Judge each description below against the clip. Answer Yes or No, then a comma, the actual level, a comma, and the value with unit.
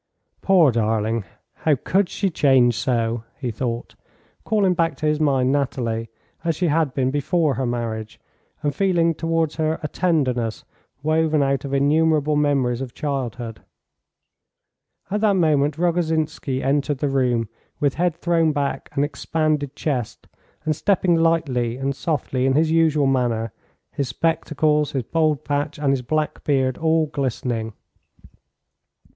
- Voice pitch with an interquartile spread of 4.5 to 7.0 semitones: No, average, 3.8 semitones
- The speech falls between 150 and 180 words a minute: No, average, 140 wpm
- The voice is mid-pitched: Yes, medium, 145 Hz